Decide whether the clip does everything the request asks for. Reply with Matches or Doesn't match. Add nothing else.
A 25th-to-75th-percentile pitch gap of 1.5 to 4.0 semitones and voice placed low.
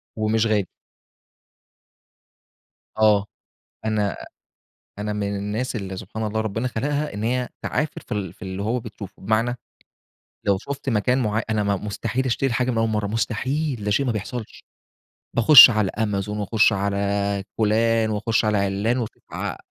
Matches